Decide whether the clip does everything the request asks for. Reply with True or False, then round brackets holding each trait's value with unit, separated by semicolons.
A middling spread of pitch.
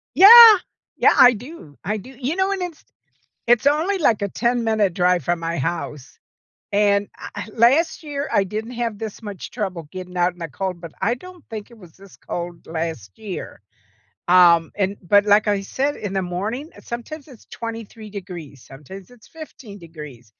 False (5.7 semitones)